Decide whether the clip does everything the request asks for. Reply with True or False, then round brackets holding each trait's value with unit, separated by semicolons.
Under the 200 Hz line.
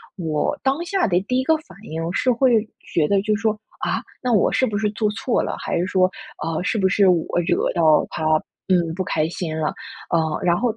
True (190 Hz)